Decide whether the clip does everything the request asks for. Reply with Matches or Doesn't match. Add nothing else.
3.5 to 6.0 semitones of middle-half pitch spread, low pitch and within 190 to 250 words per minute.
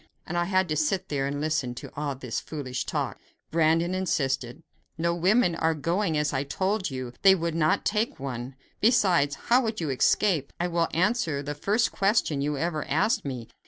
Doesn't match